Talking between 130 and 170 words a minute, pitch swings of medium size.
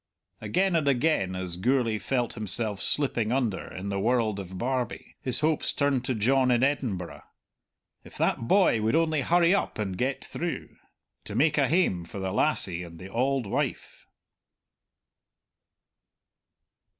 No: average, 150 wpm; wide, 6.1 semitones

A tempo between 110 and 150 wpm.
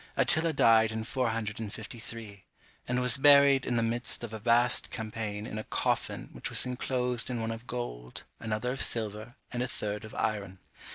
No: average, 175 wpm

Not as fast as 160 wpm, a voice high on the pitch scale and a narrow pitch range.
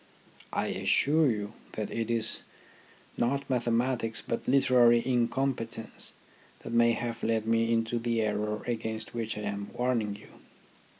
No: slow, 135 wpm; low, 115 Hz; narrow, 1.5 semitones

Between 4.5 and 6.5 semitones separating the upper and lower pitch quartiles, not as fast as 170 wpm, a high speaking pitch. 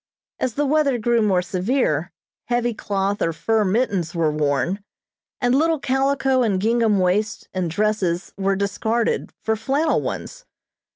Yes: average, 5.0 semitones; average, 140 wpm; high, 215 Hz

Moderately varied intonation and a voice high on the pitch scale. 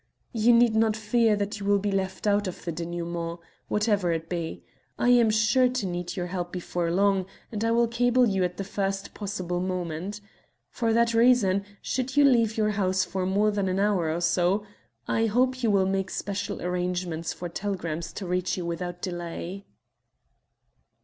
Yes: average, 3.6 semitones; high, 195 Hz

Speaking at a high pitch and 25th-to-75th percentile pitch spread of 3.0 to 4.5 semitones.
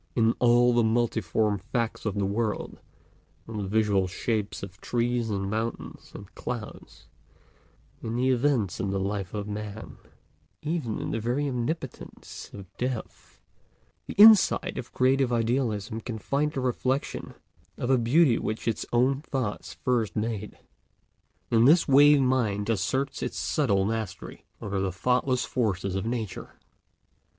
No: low, 115 Hz; average, 3.6 semitones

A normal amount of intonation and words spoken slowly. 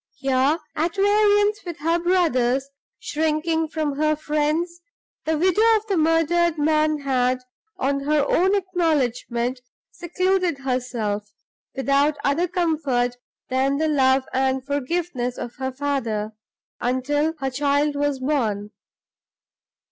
Yes: average, 4.1 semitones; slow, 115 wpm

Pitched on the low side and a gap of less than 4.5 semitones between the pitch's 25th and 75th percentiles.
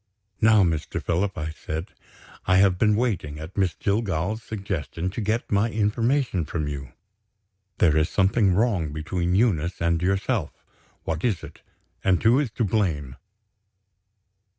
No: very low, 95 Hz; average, 4.9 semitones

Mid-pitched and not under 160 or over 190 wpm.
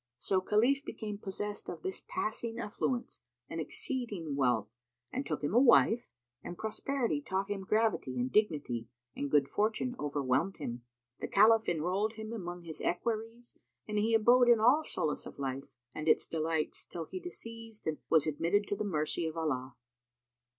No: high, 200 Hz; average, 165 wpm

